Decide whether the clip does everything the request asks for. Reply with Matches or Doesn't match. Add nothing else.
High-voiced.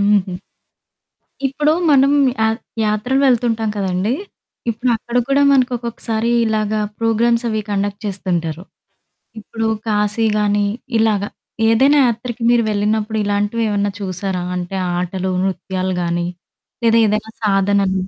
Matches